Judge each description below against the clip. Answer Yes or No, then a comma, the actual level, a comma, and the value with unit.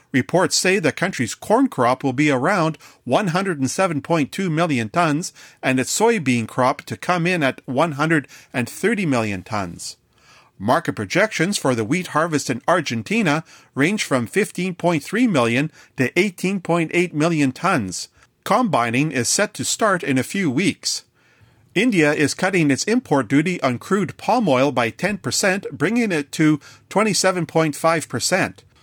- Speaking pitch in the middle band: Yes, medium, 155 Hz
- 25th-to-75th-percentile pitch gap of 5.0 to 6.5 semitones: Yes, wide, 5.6 semitones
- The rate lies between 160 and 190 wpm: No, slow, 135 wpm